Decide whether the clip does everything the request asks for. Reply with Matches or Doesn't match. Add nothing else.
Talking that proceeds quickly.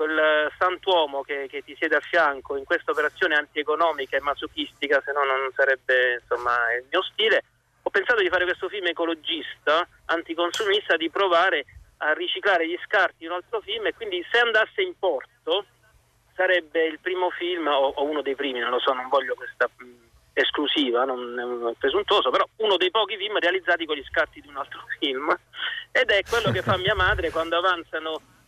Matches